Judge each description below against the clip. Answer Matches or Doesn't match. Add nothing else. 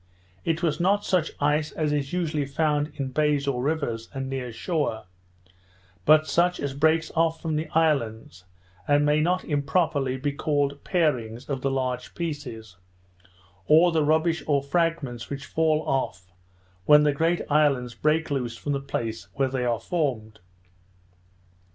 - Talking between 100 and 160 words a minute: Matches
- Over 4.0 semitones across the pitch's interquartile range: Doesn't match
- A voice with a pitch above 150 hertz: Doesn't match